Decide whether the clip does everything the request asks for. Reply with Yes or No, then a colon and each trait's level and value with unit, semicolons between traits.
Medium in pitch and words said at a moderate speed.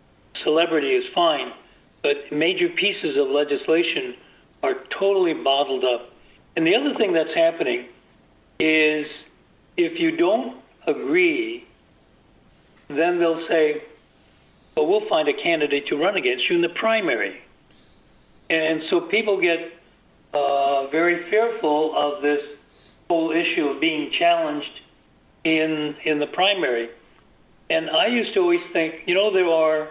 No: medium, 170 Hz; slow, 130 wpm